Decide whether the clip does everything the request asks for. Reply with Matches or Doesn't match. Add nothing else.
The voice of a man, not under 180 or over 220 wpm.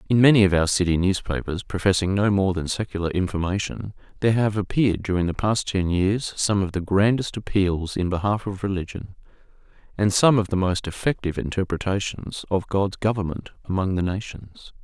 Doesn't match